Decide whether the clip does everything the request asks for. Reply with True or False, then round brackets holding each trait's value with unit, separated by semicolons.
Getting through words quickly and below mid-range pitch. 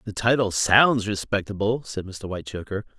False (140 wpm; 105 Hz)